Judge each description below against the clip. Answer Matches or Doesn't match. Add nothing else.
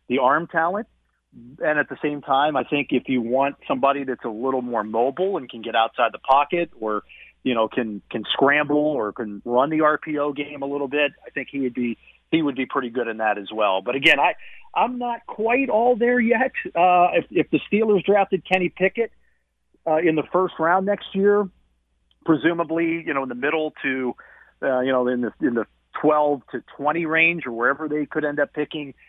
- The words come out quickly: Matches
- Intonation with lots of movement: Matches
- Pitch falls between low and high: Matches